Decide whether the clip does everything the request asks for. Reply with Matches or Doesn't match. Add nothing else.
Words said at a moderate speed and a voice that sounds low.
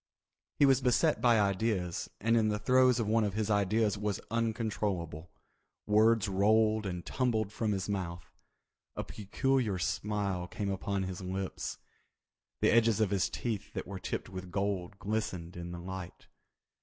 Matches